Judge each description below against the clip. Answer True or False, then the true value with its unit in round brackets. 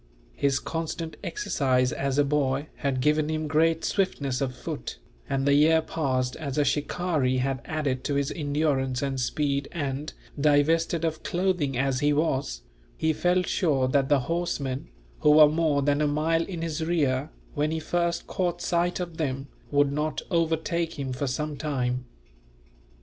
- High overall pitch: False (150 Hz)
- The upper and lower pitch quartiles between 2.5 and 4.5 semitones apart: True (3.0 semitones)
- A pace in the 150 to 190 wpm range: True (165 wpm)